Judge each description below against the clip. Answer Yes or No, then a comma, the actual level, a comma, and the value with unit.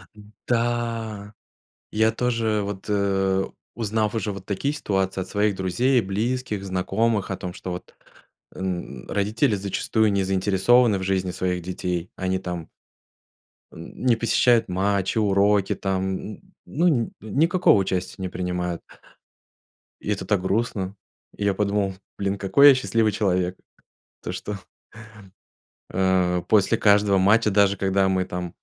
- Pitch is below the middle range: Yes, low, 100 Hz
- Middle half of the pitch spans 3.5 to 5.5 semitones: No, average, 2.7 semitones